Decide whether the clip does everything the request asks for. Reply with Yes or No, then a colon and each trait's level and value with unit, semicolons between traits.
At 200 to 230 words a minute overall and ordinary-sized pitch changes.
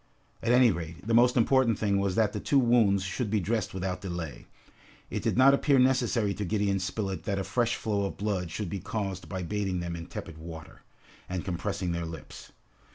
Yes: fast, 205 wpm; average, 3.8 semitones